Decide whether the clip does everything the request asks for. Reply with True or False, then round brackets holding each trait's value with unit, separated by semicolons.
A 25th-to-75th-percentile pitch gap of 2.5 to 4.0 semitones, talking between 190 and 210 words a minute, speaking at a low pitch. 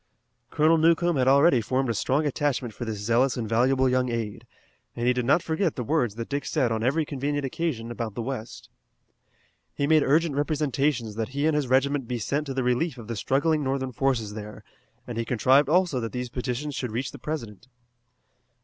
True (3.7 semitones; 205 wpm; 130 Hz)